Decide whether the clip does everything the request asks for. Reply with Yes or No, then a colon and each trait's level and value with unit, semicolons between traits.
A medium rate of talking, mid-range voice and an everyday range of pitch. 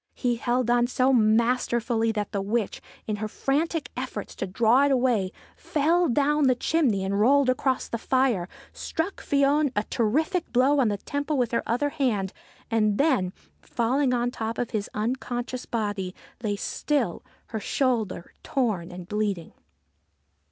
No: average, 150 wpm; high, 240 Hz; average, 4.2 semitones